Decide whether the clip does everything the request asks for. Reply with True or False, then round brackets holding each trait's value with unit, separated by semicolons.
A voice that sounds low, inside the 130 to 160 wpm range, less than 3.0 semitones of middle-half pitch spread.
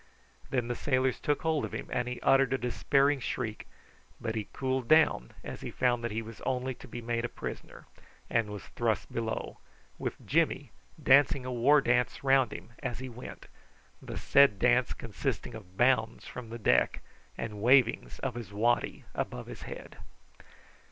False (120 Hz; 175 wpm; 2.6 semitones)